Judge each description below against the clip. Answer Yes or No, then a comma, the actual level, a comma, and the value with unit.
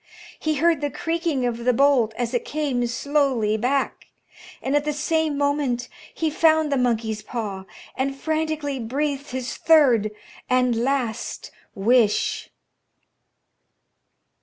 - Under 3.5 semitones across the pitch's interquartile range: No, average, 3.9 semitones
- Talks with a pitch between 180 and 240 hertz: No, very high, 270 Hz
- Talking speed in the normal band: No, slow, 125 wpm